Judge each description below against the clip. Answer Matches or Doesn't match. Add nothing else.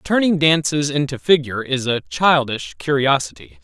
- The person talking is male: Matches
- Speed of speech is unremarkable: Doesn't match